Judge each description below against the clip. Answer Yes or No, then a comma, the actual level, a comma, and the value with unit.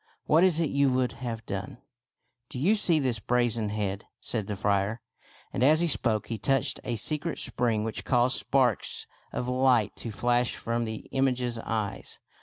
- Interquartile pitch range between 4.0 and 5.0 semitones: No, average, 3.3 semitones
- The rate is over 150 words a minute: Yes, average, 190 wpm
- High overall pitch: No, low, 120 Hz